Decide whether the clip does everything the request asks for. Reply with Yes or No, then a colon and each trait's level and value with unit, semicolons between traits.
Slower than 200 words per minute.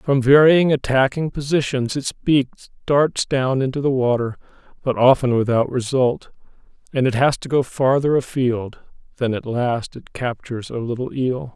Yes: average, 155 wpm